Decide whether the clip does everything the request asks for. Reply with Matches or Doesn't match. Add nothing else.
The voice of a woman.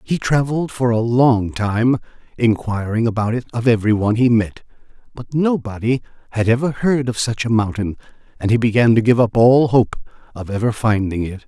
Doesn't match